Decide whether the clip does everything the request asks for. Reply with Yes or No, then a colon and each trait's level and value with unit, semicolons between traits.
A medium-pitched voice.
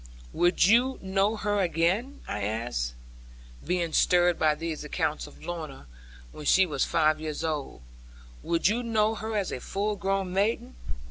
Yes: medium, 175 Hz